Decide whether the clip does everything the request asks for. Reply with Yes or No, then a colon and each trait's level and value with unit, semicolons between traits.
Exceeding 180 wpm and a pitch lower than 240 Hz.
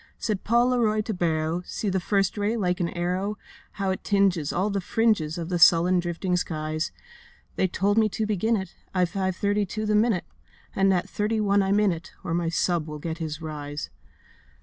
Yes: average, 200 wpm; medium, 185 Hz